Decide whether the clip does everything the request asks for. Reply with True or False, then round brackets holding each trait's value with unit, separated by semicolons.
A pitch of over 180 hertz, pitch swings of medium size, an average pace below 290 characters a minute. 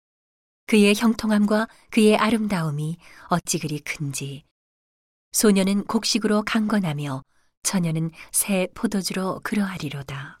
False (190 Hz; 5.7 semitones; 255 characters per minute)